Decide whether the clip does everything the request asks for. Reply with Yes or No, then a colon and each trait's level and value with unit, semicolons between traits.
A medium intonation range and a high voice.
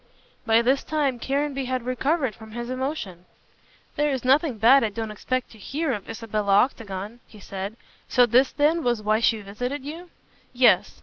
Yes: average, 4.1 semitones; high, 245 Hz